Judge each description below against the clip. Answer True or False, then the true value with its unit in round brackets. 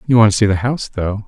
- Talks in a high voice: False (110 Hz)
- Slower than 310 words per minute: False (330 wpm)